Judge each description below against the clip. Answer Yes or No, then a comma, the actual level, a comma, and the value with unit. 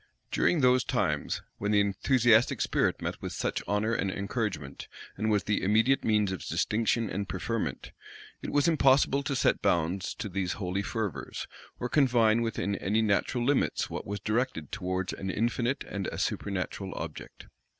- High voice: No, low, 105 Hz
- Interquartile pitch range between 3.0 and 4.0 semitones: Yes, average, 3.7 semitones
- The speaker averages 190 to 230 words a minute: No, average, 160 wpm